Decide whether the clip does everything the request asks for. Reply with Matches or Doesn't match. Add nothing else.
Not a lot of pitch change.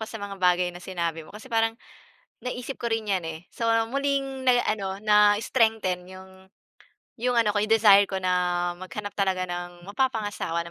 Doesn't match